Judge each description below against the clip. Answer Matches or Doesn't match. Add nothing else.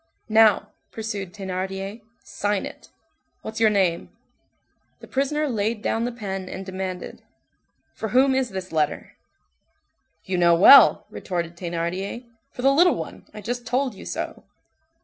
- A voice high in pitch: Matches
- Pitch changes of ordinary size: Matches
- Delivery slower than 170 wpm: Matches